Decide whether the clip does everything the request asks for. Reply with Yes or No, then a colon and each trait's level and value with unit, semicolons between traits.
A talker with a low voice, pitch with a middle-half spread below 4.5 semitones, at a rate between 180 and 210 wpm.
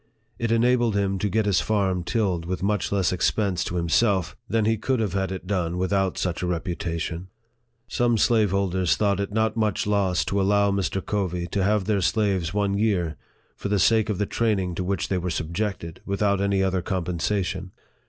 Yes: low, 100 Hz; narrow, 2.4 semitones; average, 190 wpm